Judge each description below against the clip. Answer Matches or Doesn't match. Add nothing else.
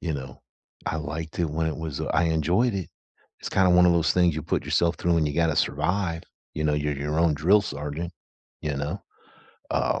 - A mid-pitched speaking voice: Doesn't match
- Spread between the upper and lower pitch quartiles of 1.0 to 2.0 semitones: Doesn't match